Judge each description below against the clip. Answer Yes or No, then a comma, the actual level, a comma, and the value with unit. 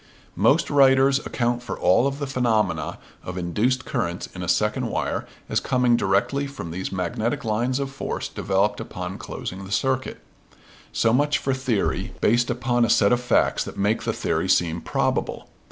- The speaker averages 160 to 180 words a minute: Yes, average, 170 wpm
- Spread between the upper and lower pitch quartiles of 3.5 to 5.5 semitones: Yes, average, 4.7 semitones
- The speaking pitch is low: Yes, low, 120 Hz